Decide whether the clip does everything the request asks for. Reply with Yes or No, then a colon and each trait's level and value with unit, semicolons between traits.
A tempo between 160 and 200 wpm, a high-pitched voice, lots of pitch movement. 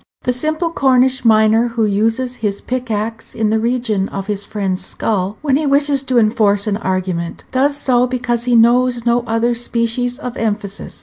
No: average, 175 wpm; high, 235 Hz; average, 2.9 semitones